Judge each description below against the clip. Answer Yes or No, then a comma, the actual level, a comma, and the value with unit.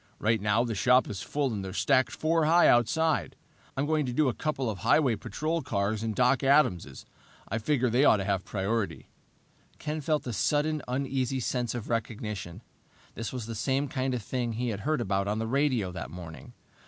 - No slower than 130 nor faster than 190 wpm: No, average, 200 wpm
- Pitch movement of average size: Yes, average, 4.8 semitones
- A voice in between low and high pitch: No, low, 120 Hz